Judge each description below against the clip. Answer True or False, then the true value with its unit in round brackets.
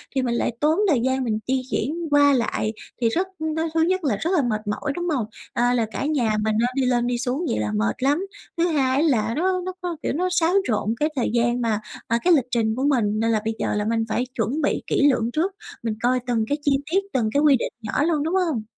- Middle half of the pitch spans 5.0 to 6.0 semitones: True (5.5 semitones)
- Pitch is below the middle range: False (260 Hz)